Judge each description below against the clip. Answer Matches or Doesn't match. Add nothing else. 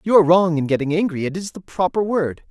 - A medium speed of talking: Doesn't match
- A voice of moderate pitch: Matches